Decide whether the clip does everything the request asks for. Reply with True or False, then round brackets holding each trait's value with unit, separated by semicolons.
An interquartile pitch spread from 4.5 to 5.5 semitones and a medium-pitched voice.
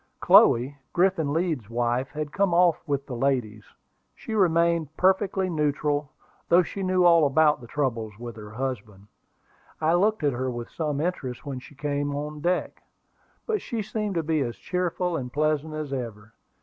True (5.2 semitones; 150 Hz)